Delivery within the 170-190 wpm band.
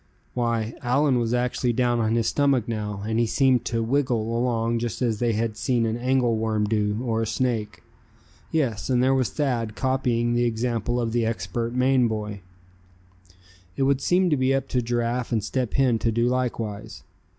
Yes: average, 185 wpm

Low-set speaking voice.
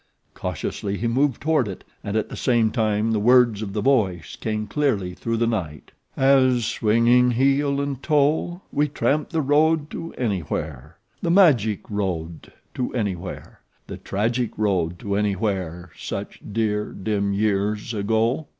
Yes: low, 110 Hz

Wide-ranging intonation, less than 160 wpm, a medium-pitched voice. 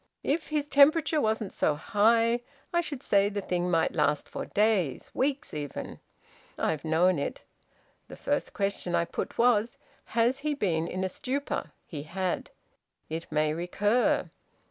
No: wide, 6.8 semitones; average, 150 wpm; high, 205 Hz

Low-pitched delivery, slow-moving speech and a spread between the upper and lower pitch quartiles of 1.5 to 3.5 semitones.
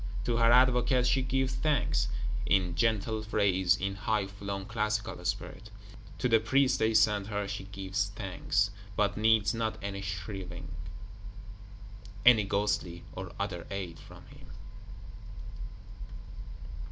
Yes: low, 105 Hz; slow, 125 wpm; narrow, 2.6 semitones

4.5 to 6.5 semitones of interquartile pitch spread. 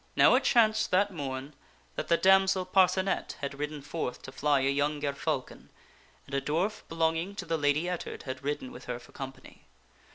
Yes: average, 5.1 semitones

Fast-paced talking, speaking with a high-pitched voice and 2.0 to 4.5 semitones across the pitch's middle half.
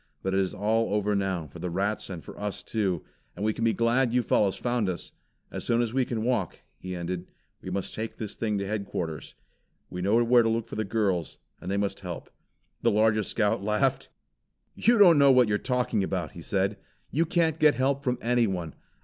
No: fast, 215 wpm; low, 105 Hz; average, 3.8 semitones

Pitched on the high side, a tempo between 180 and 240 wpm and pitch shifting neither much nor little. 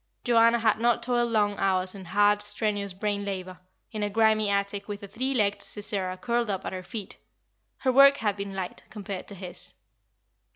No: high, 205 Hz; average, 190 wpm; narrow, 2.3 semitones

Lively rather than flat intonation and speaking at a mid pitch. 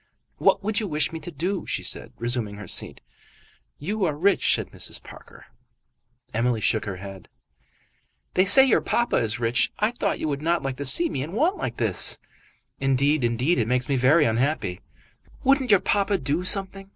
Yes: wide, 8.1 semitones; medium, 150 Hz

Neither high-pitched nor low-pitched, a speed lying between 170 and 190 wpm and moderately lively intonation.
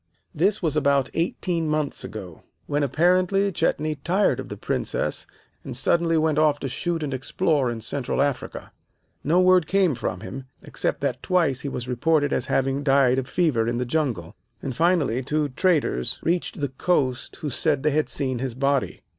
Yes: medium, 145 Hz; average, 180 wpm; average, 4.1 semitones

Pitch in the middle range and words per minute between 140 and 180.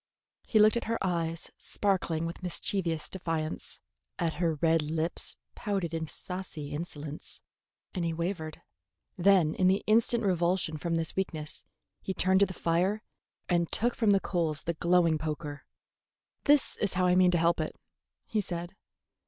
Yes: medium, 175 Hz; average, 160 wpm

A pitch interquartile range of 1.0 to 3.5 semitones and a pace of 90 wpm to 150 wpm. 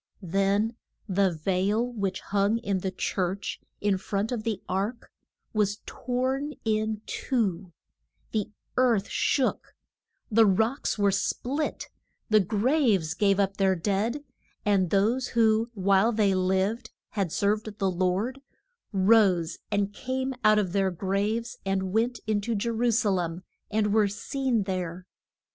Yes: average, 3.0 semitones; average, 140 wpm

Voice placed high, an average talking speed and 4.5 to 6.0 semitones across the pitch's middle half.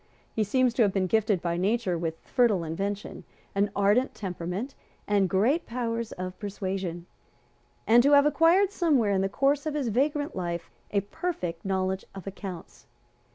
Yes: high, 205 Hz; average, 160 wpm; average, 5.2 semitones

